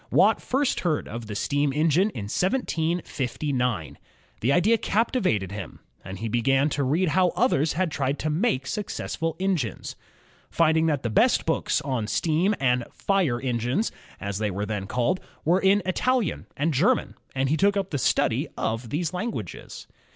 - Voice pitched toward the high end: No, medium, 150 Hz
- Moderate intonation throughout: No, wide, 7.5 semitones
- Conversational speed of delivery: Yes, average, 160 wpm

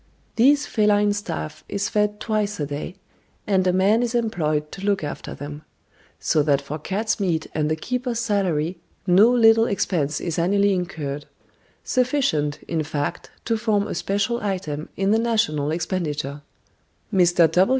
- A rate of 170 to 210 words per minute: No, average, 150 wpm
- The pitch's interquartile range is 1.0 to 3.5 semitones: No, wide, 5.6 semitones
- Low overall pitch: No, high, 190 Hz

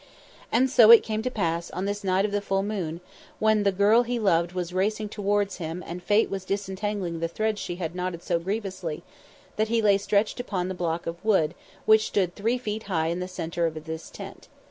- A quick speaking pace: Yes, fast, 215 wpm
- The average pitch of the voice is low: No, high, 195 Hz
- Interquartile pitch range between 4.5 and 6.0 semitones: No, average, 3.6 semitones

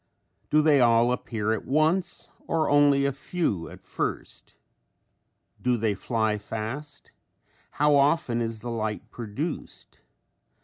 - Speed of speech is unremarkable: No, slow, 125 wpm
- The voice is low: Yes, low, 125 Hz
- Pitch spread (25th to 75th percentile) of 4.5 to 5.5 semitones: Yes, average, 4.9 semitones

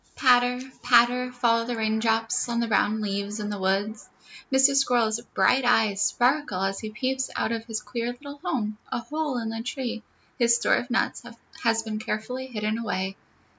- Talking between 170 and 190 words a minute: Yes, average, 175 wpm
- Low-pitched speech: No, high, 230 Hz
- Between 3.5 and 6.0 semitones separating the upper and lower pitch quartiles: No, narrow, 2.4 semitones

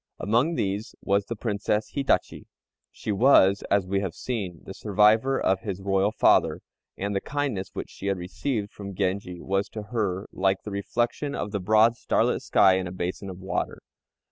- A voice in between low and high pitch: No, low, 100 Hz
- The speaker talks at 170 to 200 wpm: Yes, average, 180 wpm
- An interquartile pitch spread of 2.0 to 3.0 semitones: Yes, narrow, 2.4 semitones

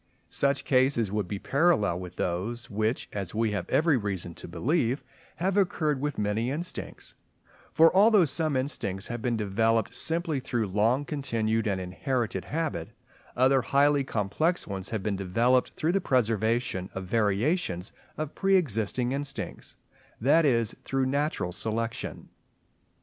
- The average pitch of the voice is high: No, low, 120 Hz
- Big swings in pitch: Yes, wide, 5.8 semitones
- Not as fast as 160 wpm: Yes, average, 140 wpm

